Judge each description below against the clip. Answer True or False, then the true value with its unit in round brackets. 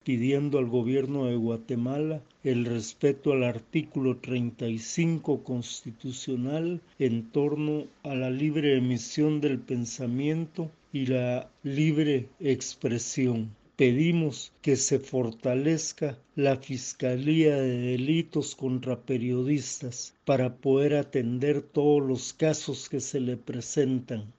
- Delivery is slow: True (105 wpm)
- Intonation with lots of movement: False (2.8 semitones)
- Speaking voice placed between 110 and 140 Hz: True (135 Hz)